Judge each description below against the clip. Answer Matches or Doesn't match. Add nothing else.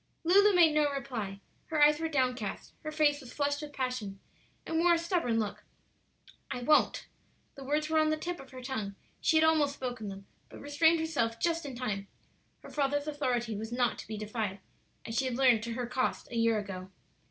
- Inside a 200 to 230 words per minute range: Matches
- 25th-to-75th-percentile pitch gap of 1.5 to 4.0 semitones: Doesn't match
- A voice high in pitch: Matches